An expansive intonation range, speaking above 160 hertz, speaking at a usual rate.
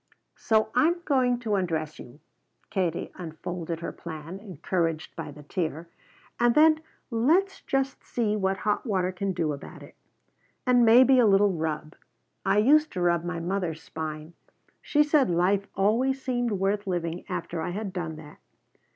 Yes: wide, 6.1 semitones; high, 190 Hz; average, 160 wpm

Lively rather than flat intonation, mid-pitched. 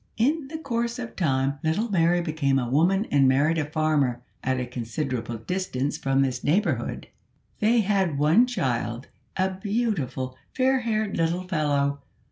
Yes: wide, 7.4 semitones; medium, 155 Hz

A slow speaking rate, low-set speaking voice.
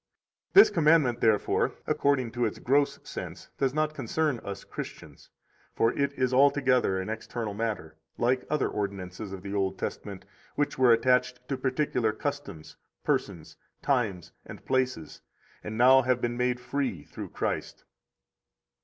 No: average, 145 wpm; low, 125 Hz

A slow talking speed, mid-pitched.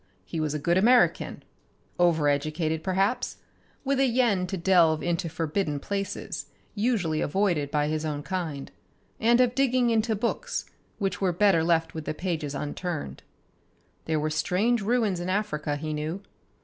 No: average, 155 wpm; medium, 175 Hz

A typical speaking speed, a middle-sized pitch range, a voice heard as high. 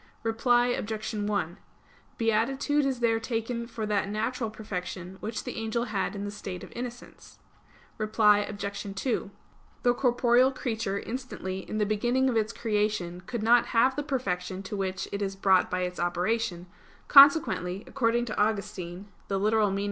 Yes: average, 155 wpm; average, 3.3 semitones; high, 215 Hz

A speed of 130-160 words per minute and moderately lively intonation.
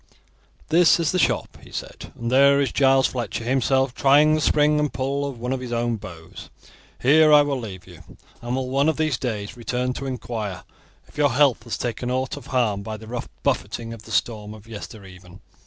No: fast, 205 wpm; average, 3.6 semitones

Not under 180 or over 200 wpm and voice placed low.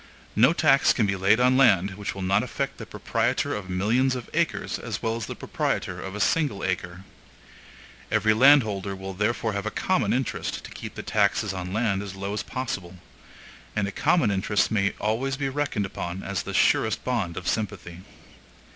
Yes: average, 185 wpm; low, 105 Hz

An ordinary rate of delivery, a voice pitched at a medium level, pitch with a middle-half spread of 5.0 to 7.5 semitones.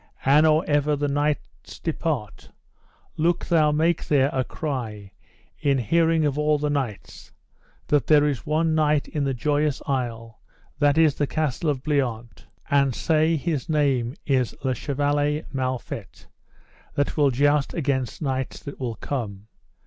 No: average, 150 wpm; medium, 145 Hz; narrow, 2.6 semitones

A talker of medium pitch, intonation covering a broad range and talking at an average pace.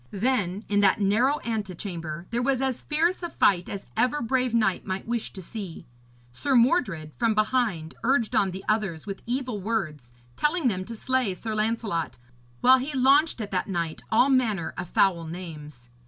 No: high, 215 Hz; wide, 5.7 semitones; average, 175 wpm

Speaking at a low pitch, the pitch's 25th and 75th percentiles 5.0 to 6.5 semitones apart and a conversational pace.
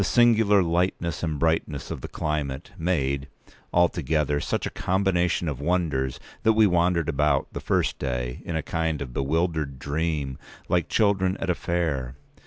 No: very low, 80 Hz; average, 4.0 semitones; average, 150 wpm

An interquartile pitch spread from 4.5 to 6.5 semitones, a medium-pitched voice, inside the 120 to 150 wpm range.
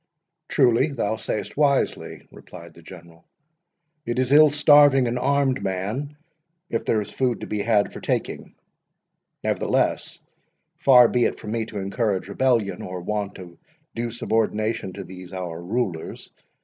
No: average, 5.0 semitones; low, 110 Hz; average, 145 wpm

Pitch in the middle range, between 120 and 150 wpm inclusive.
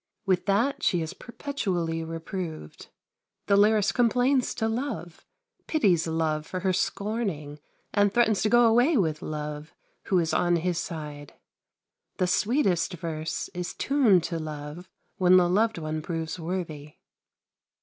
Yes: medium, 180 Hz; average, 140 wpm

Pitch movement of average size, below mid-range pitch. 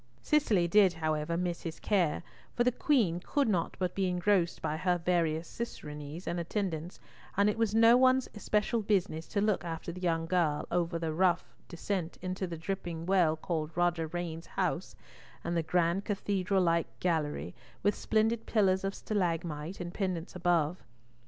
No: average, 3.3 semitones; medium, 175 Hz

